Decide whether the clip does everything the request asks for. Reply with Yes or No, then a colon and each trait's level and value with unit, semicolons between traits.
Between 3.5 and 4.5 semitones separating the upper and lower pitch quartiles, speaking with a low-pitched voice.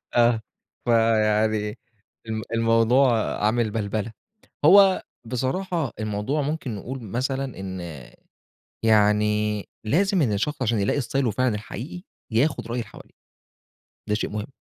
Yes: average, 3.9 semitones; low, 115 Hz